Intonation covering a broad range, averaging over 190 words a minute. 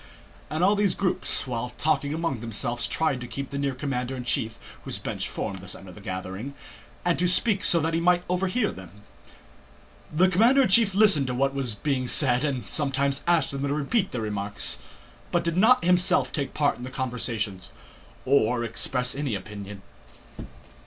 No: wide, 6.7 semitones; average, 185 wpm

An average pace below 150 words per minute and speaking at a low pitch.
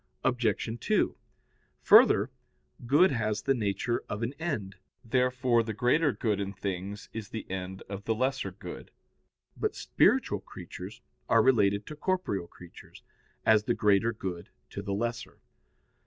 Yes: average, 140 wpm; low, 110 Hz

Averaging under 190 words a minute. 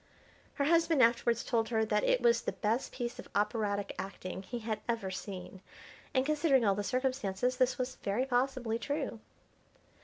Yes: average, 165 wpm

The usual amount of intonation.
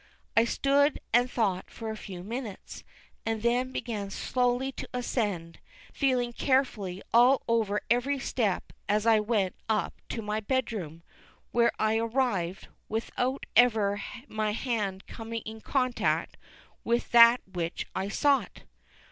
Yes: average, 3.2 semitones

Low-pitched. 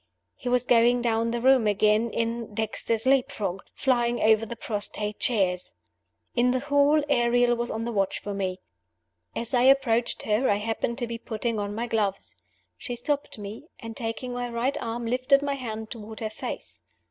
No: high, 235 Hz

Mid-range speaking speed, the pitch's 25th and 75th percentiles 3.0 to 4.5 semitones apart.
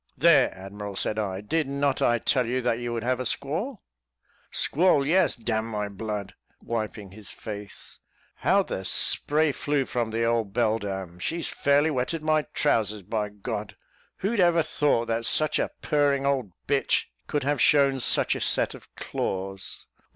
No: average, 170 wpm; wide, 5.5 semitones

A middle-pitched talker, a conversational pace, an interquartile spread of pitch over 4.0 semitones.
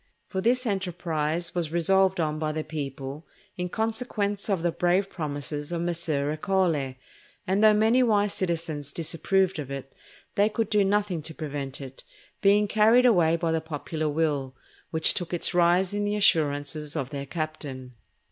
Yes: medium, 170 Hz; average, 165 wpm; average, 4.5 semitones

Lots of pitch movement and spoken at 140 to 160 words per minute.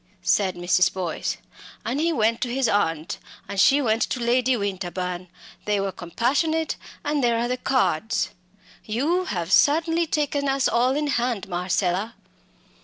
Yes: wide, 6.4 semitones; average, 150 wpm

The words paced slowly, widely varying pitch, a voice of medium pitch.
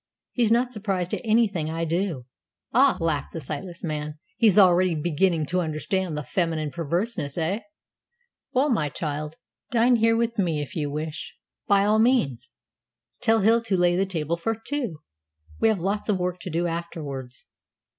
No: average, 165 wpm; wide, 5.7 semitones; medium, 175 Hz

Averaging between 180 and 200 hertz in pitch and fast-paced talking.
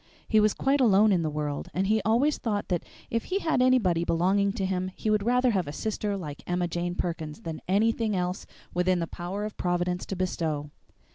Yes: high, 190 Hz; fast, 210 wpm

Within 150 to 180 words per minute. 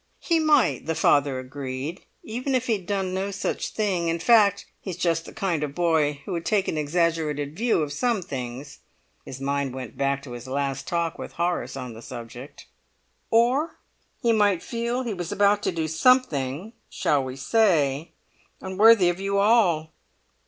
Yes: average, 175 wpm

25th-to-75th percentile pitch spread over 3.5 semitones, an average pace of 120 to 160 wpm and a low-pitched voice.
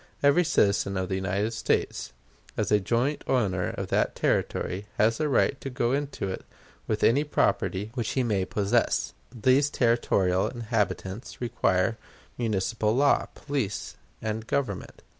Yes: average, 4.5 semitones; average, 140 wpm; low, 115 Hz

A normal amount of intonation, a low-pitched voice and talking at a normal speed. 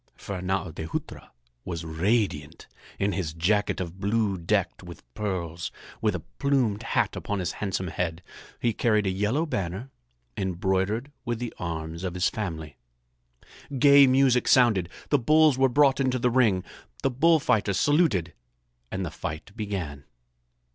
No: wide, 5.8 semitones; low, 100 Hz; average, 145 wpm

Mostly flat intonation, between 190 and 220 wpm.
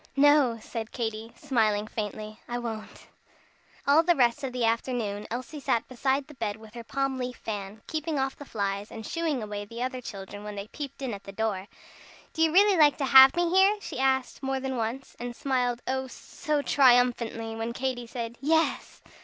No: average, 3.6 semitones; average, 195 wpm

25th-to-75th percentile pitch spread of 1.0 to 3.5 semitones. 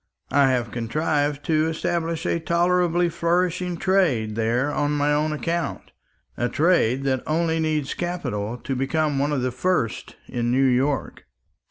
No: average, 4.6 semitones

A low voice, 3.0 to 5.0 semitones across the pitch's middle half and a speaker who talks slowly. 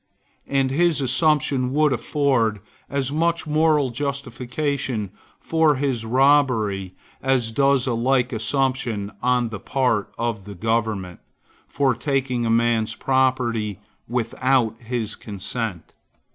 Yes: low, 125 Hz; average, 3.6 semitones; slow, 115 wpm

